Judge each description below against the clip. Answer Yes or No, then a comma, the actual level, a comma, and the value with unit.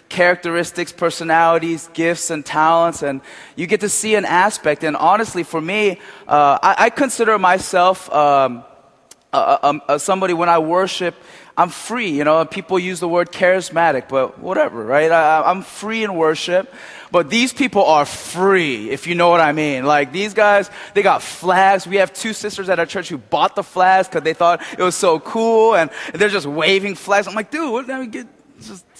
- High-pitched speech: No, medium, 180 Hz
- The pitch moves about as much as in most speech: Yes, average, 3.6 semitones